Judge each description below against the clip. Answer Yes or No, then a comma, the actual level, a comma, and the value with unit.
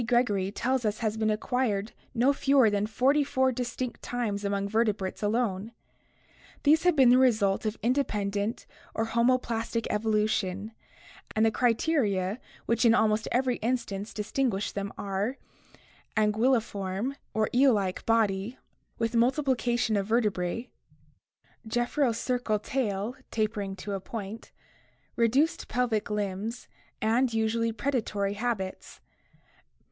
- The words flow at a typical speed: No, slow, 115 wpm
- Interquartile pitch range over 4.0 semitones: No, average, 3.3 semitones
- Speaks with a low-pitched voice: No, high, 225 Hz